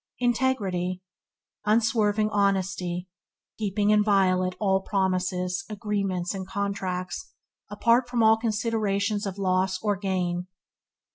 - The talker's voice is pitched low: No, high, 200 Hz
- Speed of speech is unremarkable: No, slow, 100 wpm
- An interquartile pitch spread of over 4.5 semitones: No, narrow, 2.6 semitones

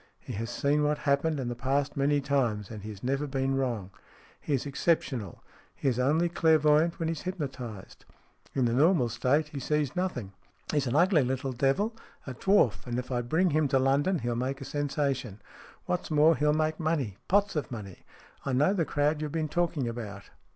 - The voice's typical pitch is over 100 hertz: Yes, medium, 140 Hz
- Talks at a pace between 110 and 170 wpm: No, average, 200 wpm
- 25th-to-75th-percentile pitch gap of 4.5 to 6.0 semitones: No, average, 3.8 semitones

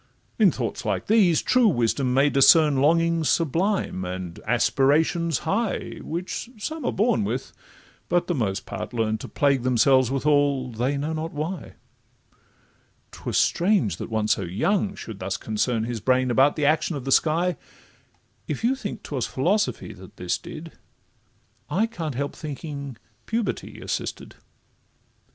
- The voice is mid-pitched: Yes, medium, 145 Hz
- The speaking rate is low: No, average, 145 wpm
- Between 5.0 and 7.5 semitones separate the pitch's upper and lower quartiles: Yes, wide, 5.6 semitones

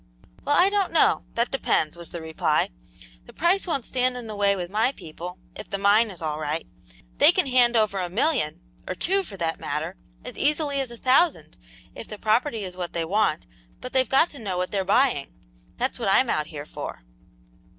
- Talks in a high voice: Yes, high, 215 Hz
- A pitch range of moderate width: No, wide, 6.9 semitones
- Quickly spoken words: Yes, fast, 210 wpm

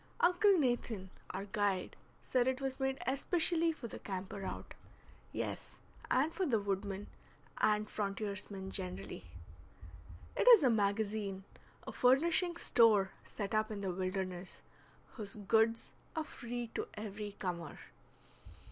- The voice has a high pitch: Yes, high, 215 Hz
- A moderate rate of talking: No, slow, 130 wpm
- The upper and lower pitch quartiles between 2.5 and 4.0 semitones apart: No, average, 4.9 semitones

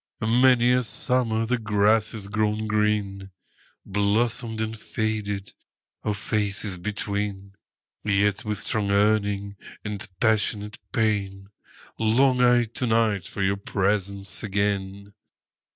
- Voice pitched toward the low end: Yes, low, 105 Hz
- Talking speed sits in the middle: No, slow, 100 wpm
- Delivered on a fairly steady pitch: Yes, narrow, 1.8 semitones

